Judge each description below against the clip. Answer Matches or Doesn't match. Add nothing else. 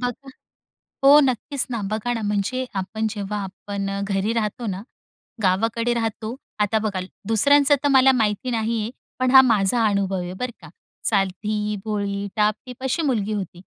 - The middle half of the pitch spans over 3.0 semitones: Matches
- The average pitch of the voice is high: Matches